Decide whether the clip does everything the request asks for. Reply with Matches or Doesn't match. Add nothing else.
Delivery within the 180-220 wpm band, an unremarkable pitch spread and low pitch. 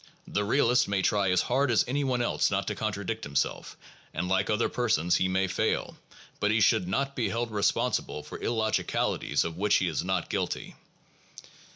Matches